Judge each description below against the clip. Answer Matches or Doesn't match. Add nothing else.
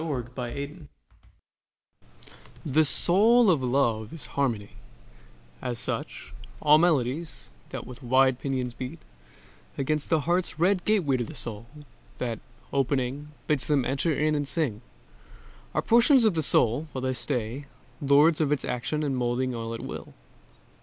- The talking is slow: Doesn't match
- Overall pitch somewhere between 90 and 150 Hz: Matches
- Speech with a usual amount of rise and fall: Matches